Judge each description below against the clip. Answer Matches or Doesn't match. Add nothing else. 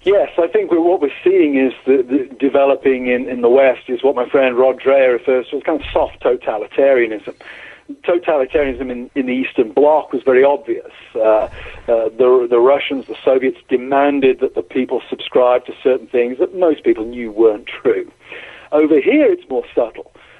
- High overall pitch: Doesn't match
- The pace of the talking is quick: Doesn't match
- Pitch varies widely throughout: Matches